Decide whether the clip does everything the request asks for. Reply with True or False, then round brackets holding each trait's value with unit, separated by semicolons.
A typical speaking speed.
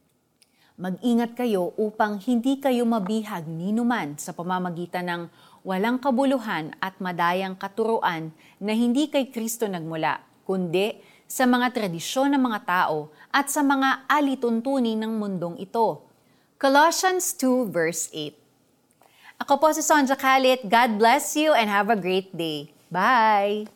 True (130 wpm)